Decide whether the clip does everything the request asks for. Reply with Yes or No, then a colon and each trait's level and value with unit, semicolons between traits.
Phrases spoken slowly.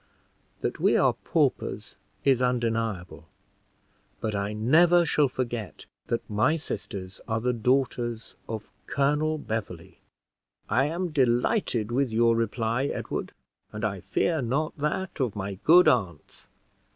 Yes: slow, 125 wpm